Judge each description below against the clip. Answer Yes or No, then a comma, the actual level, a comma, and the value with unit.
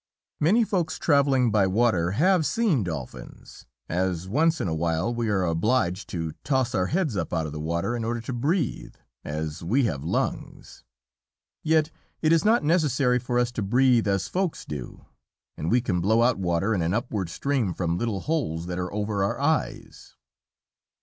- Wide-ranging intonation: Yes, wide, 8.0 semitones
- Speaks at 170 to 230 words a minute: Yes, average, 175 wpm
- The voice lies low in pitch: Yes, low, 115 Hz